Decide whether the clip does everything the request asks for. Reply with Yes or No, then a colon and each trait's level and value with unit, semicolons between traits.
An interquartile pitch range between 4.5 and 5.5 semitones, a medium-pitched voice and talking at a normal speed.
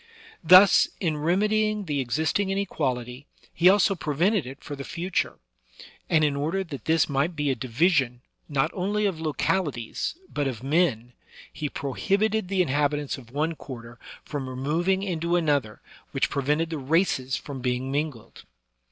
Yes: average, 5.2 semitones; medium, 150 Hz; average, 155 wpm